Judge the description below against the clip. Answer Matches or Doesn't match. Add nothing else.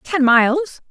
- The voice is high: Matches